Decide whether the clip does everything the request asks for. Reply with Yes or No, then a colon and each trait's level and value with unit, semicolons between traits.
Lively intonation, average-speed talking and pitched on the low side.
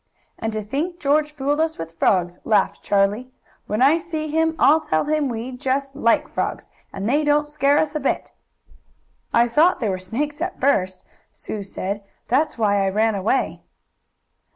No: wide, 6.3 semitones; average, 175 wpm; very high, 260 Hz